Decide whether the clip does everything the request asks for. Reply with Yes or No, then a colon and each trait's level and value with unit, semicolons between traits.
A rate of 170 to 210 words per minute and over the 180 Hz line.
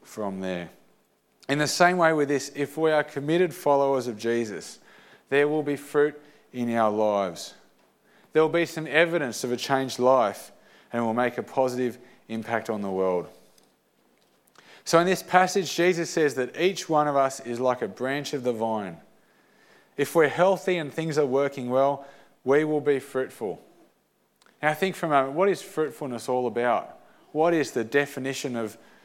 No: average, 180 wpm; medium, 140 Hz